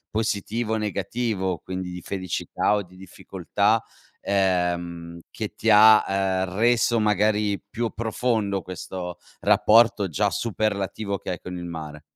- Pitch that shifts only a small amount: No, average, 3.1 semitones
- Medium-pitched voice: No, low, 100 Hz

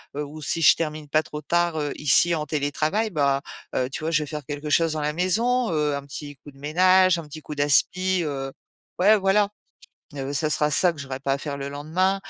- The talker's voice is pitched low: No, medium, 150 Hz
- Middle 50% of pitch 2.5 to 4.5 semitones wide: Yes, average, 3.3 semitones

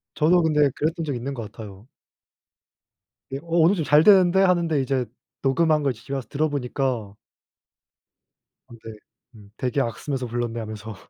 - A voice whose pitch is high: No, low, 135 Hz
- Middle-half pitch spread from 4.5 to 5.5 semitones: Yes, average, 5.1 semitones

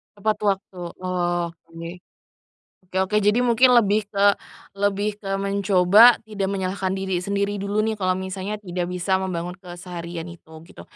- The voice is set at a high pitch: Yes, high, 195 Hz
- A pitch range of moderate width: No, narrow, 2.1 semitones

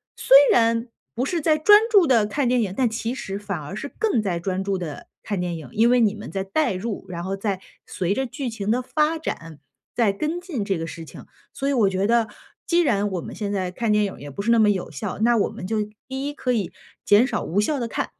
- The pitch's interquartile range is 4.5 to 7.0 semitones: Yes, average, 4.8 semitones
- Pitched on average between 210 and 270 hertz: Yes, high, 215 Hz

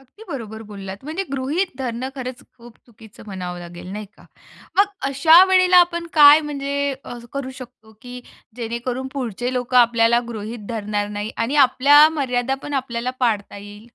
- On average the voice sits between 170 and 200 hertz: No, high, 245 Hz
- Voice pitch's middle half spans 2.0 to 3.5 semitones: No, average, 4.1 semitones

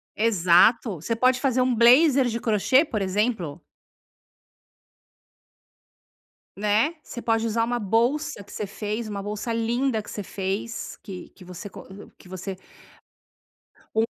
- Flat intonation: No, average, 3.2 semitones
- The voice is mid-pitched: No, high, 225 Hz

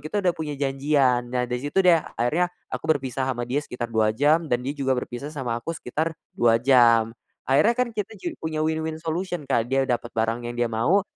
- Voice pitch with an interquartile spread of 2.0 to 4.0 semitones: No, average, 4.7 semitones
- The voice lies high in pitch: No, low, 135 Hz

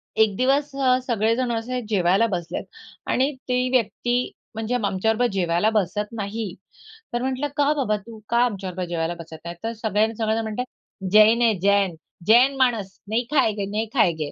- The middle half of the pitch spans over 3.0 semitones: Yes, average, 3.9 semitones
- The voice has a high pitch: Yes, high, 220 Hz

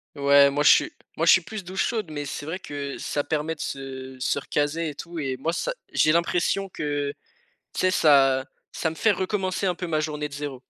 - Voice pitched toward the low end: No, medium, 150 Hz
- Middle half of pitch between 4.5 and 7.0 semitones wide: No, average, 3.7 semitones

